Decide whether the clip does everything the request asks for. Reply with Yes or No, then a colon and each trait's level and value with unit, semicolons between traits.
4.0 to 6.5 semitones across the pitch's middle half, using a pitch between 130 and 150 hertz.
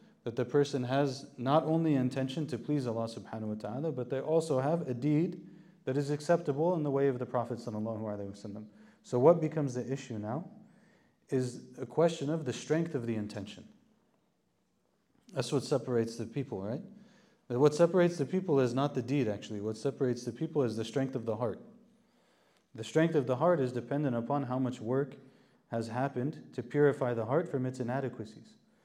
Yes: average, 4.8 semitones; low, 135 Hz